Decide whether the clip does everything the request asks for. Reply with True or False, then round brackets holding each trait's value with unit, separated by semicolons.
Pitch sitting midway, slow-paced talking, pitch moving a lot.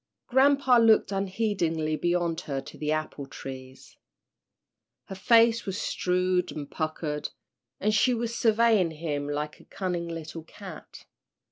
True (175 Hz; 130 wpm; 5.8 semitones)